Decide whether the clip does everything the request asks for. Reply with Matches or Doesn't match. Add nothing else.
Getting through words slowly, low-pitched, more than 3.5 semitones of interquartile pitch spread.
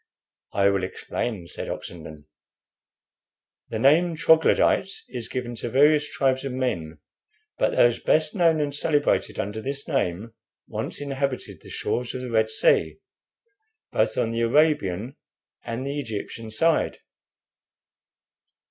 Matches